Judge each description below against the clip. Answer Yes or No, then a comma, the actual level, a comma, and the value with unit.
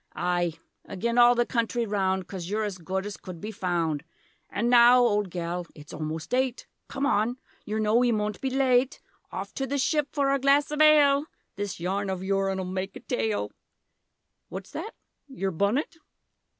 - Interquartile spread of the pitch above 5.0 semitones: Yes, wide, 5.4 semitones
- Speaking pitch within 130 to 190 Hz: No, high, 210 Hz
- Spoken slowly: No, average, 175 wpm